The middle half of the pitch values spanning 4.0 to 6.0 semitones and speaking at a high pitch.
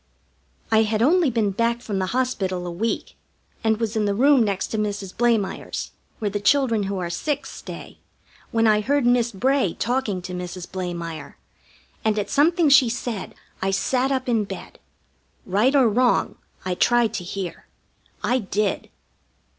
Yes: average, 4.4 semitones; high, 220 Hz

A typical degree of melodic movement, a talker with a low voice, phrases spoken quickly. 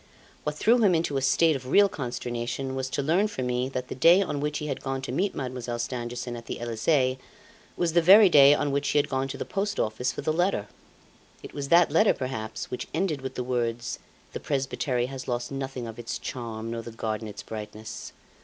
Yes: average, 3.7 semitones; low, 130 Hz; fast, 220 wpm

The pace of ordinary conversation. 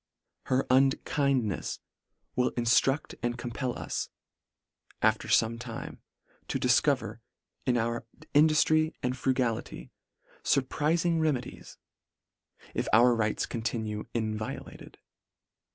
No: slow, 100 wpm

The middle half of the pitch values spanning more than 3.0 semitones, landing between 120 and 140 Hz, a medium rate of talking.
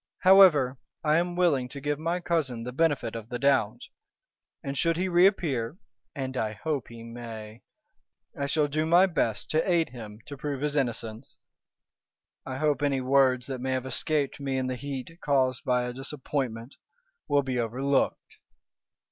Yes: average, 3.6 semitones; low, 135 Hz; average, 165 wpm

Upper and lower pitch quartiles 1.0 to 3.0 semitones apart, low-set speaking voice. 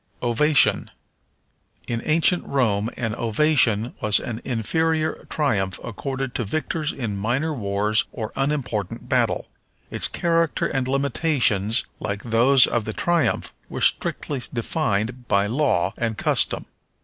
No: wide, 5.4 semitones; low, 120 Hz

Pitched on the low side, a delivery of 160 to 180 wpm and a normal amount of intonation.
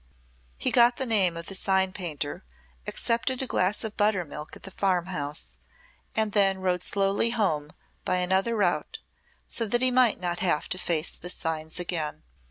No: high, 190 Hz; average, 175 wpm; average, 3.9 semitones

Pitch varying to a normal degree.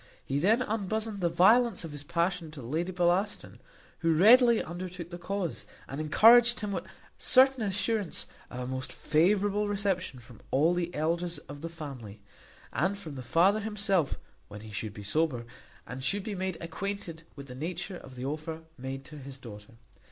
No: wide, 6.0 semitones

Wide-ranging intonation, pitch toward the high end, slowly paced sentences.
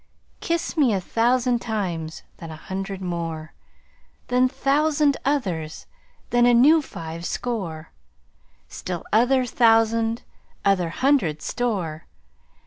Yes: wide, 6.9 semitones; high, 225 Hz; slow, 105 wpm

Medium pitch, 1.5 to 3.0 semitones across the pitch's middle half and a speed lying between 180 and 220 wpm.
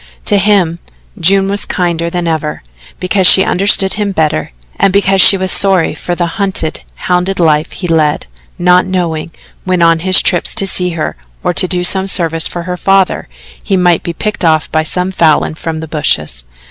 Yes: medium, 180 Hz; average, 2.7 semitones; average, 185 wpm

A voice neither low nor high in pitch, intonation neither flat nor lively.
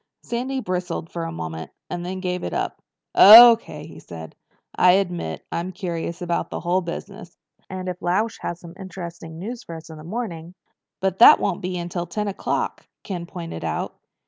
No: medium, 180 Hz; narrow, 2.3 semitones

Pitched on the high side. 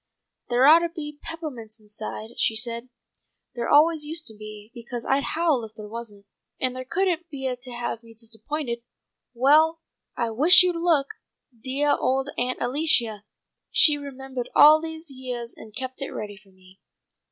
Yes: very high, 255 Hz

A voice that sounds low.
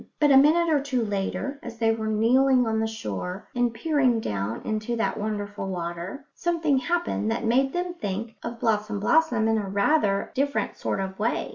No: high, 225 Hz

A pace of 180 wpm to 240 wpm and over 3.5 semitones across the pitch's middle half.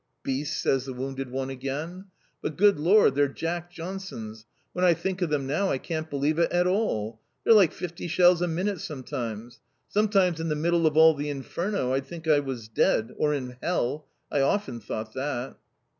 Yes: average, 190 wpm; average, 4.8 semitones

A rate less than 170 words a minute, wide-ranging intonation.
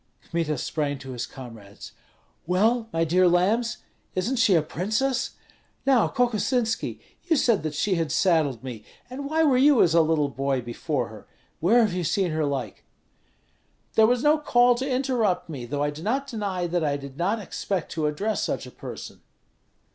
No: average, 180 wpm; wide, 8.0 semitones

